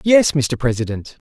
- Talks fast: No, average, 140 wpm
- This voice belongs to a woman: No, male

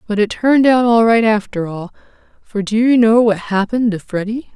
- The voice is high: Yes, high, 220 Hz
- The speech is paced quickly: Yes, fast, 210 wpm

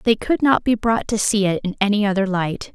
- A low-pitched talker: No, high, 205 Hz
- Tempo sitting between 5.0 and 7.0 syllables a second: Yes, 5.5 syllables/s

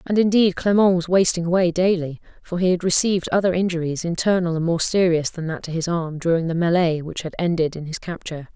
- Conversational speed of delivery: No, fast, 215 wpm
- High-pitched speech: No, medium, 175 Hz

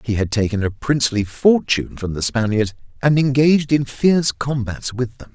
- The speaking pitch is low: Yes, low, 125 Hz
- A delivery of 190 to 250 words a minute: No, average, 180 wpm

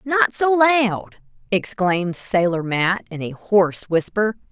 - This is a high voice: Yes, high, 205 Hz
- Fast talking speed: No, slow, 135 wpm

